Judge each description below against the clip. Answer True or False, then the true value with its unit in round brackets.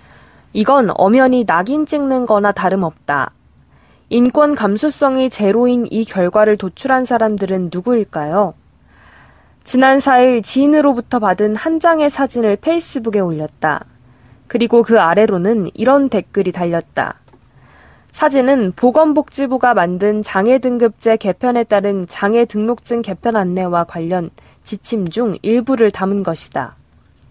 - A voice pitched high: True (220 Hz)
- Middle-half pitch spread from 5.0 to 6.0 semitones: True (5.5 semitones)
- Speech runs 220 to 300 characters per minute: True (275 characters per minute)